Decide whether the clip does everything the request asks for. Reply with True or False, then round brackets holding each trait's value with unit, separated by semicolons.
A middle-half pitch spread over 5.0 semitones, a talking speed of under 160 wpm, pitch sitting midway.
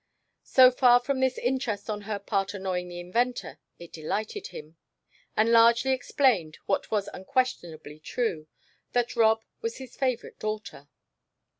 False (5.5 semitones; 140 wpm; 220 Hz)